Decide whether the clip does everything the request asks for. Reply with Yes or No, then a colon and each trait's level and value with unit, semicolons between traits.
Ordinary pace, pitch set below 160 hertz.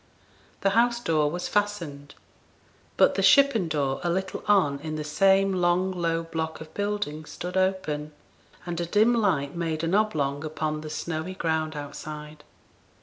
No: average, 155 wpm; medium, 165 Hz